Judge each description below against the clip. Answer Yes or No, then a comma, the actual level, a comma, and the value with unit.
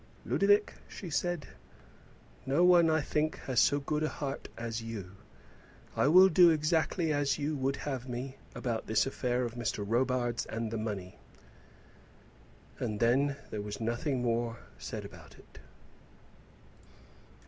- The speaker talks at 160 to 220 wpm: No, average, 140 wpm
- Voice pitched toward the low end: Yes, low, 130 Hz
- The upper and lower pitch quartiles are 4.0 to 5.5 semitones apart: Yes, average, 4.8 semitones